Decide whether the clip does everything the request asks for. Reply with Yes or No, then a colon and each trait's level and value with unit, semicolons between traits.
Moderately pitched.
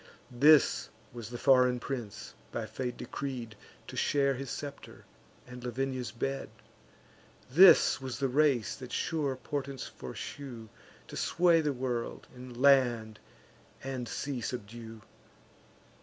No: low, 130 Hz